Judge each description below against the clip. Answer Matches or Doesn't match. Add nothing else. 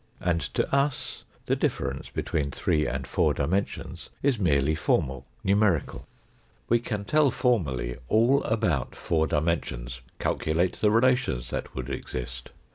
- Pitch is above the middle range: Doesn't match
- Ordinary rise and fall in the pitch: Doesn't match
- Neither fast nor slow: Doesn't match